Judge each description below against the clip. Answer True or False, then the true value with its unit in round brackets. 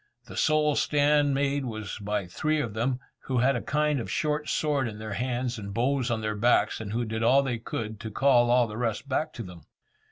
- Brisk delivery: True (225 wpm)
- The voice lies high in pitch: False (120 Hz)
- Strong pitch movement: False (4.3 semitones)